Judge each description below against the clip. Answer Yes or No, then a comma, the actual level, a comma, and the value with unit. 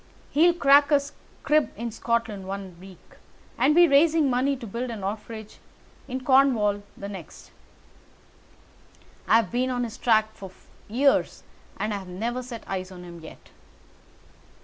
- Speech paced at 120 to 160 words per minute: Yes, average, 145 wpm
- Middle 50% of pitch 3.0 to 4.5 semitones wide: No, average, 5.1 semitones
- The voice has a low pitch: No, high, 230 Hz